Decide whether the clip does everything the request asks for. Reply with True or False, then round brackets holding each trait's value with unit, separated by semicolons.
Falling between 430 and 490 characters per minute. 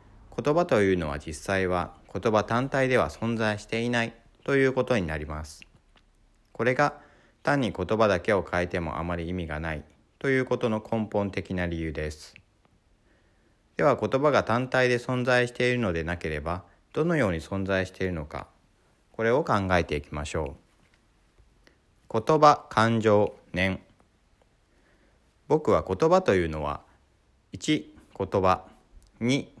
False (270 characters per minute)